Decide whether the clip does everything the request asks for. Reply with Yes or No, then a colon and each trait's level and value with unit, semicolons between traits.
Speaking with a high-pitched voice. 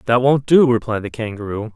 No: low, 120 Hz